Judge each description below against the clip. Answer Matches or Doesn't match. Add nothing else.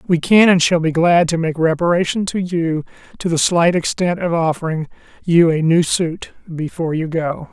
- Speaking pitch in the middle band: Matches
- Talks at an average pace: Matches